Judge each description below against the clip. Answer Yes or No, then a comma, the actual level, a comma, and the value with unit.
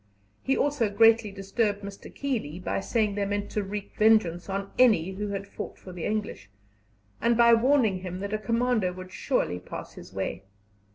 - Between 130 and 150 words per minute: No, average, 180 wpm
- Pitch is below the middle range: No, high, 205 Hz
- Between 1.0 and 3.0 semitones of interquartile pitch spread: No, average, 3.5 semitones